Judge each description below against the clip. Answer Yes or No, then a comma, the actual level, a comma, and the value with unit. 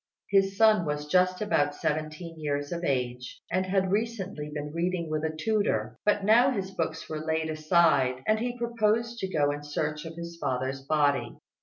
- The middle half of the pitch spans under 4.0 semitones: No, average, 4.8 semitones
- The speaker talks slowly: No, average, 180 wpm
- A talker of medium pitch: Yes, medium, 165 Hz